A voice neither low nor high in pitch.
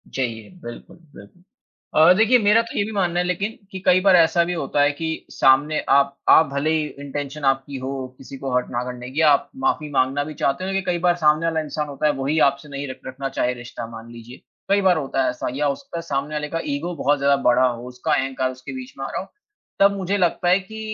Yes: medium, 145 Hz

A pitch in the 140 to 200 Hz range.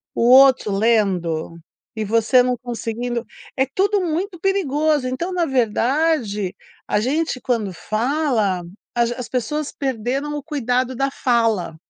No: very high, 250 Hz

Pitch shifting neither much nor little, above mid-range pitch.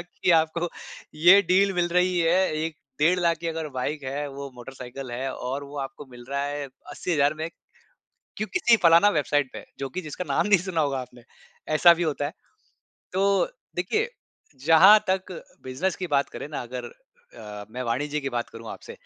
No: average, 4.7 semitones; medium, 150 Hz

